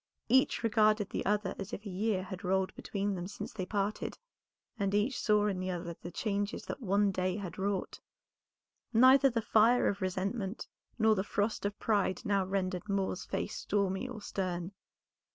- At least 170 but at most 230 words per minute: Yes, average, 175 wpm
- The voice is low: No, high, 200 Hz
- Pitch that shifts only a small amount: Yes, narrow, 2.2 semitones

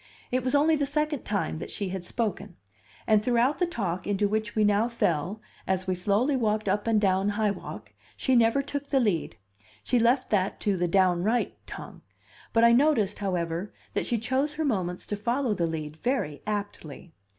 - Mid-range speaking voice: No, high, 210 Hz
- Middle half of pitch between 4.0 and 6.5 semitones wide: Yes, average, 4.7 semitones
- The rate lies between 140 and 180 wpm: No, average, 190 wpm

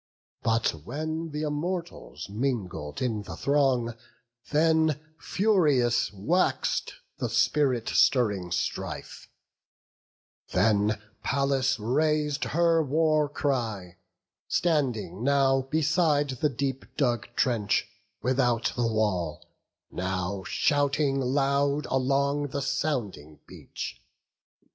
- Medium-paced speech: No, slow, 90 wpm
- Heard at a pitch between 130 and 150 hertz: Yes, low, 135 Hz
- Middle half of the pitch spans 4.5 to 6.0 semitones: Yes, average, 5.0 semitones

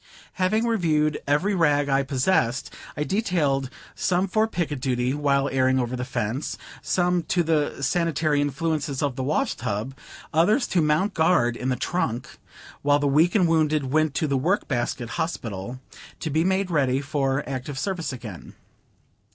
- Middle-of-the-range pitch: Yes, medium, 145 Hz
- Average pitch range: Yes, average, 4.4 semitones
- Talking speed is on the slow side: No, average, 160 wpm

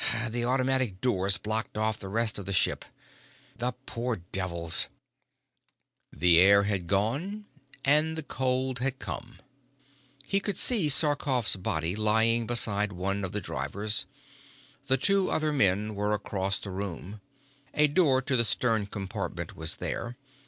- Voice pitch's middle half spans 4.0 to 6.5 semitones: Yes, average, 5.0 semitones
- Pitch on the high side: No, low, 110 Hz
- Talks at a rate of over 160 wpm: No, average, 145 wpm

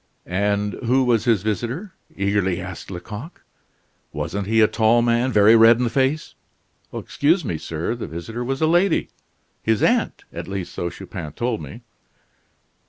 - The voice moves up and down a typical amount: Yes, average, 3.9 semitones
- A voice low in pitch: Yes, low, 110 Hz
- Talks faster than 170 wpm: No, average, 165 wpm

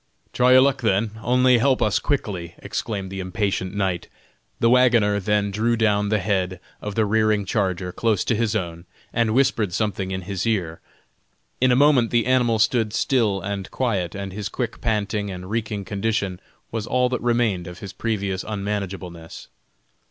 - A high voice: No, low, 105 Hz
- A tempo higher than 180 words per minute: No, average, 170 wpm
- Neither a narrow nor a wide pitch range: Yes, average, 3.2 semitones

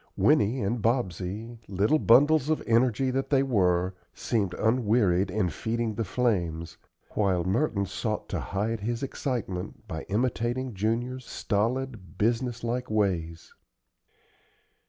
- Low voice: Yes, low, 110 Hz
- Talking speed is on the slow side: Yes, slow, 120 wpm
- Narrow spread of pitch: No, average, 4.3 semitones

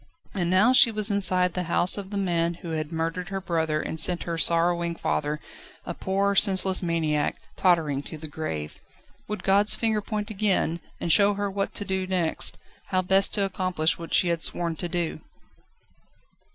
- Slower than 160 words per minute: No, average, 180 wpm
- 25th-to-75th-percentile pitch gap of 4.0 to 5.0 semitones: No, average, 2.9 semitones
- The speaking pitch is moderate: Yes, medium, 180 Hz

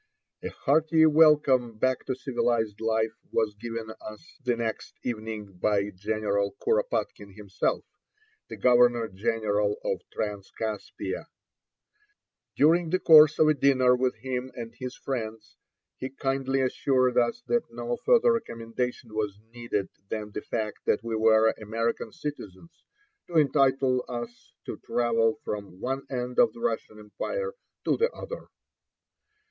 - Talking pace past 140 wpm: No, slow, 135 wpm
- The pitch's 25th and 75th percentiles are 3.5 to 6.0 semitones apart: Yes, average, 3.8 semitones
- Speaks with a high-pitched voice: No, low, 120 Hz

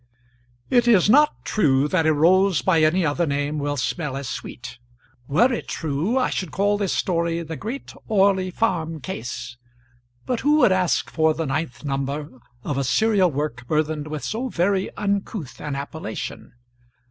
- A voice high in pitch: No, medium, 165 Hz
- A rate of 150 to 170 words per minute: Yes, average, 165 wpm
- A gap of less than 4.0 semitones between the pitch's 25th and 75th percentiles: No, wide, 5.5 semitones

